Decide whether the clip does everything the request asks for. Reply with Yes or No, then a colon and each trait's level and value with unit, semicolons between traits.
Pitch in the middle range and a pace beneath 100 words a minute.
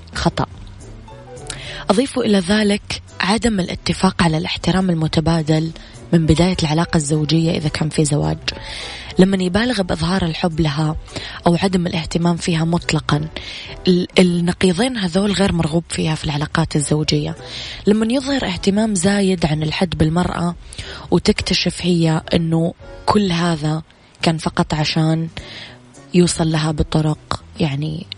No: medium, 165 Hz; average, 115 wpm